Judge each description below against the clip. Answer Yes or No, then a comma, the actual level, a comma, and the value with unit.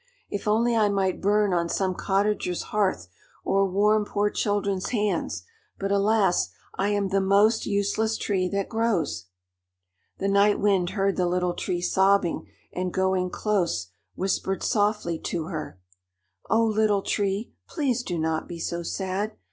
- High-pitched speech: Yes, high, 195 Hz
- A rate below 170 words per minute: Yes, average, 150 wpm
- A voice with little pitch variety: Yes, narrow, 2.3 semitones